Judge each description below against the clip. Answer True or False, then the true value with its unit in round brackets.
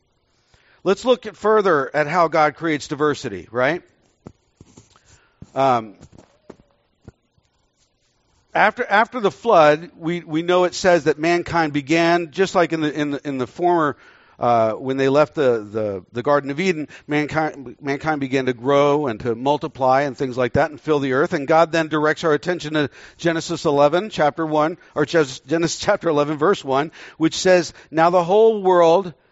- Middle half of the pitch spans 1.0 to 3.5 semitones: True (3.1 semitones)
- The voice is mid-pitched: True (150 Hz)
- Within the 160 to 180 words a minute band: True (165 wpm)